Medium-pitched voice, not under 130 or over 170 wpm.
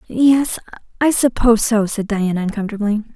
No: high, 220 Hz; slow, 135 wpm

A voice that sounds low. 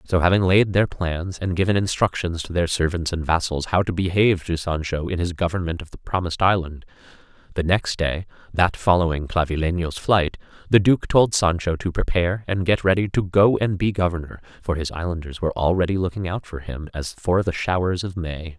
Yes: very low, 90 Hz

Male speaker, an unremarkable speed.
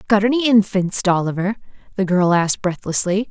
No: female; average, 145 wpm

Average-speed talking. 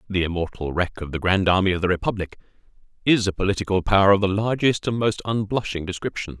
Yes: average, 195 wpm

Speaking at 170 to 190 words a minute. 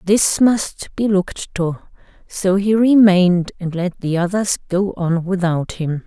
No: average, 160 wpm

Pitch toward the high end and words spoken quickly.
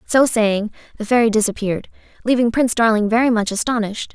No: high, 225 Hz; average, 160 wpm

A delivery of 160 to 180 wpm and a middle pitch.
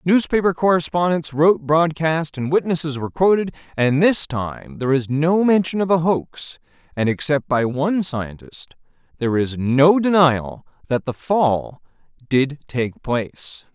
No: average, 145 wpm; medium, 150 Hz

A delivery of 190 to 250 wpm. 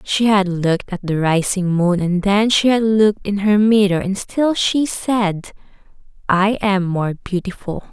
No: average, 175 wpm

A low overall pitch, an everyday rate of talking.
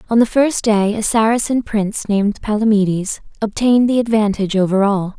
No: high, 215 Hz; average, 160 wpm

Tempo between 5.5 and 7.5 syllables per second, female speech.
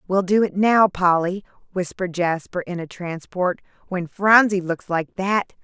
No: 4.4 syllables/s; female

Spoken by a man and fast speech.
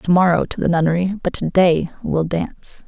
No: female; fast, 210 wpm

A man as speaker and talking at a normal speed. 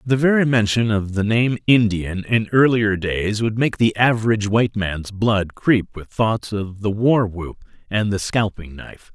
Yes: male; average, 185 wpm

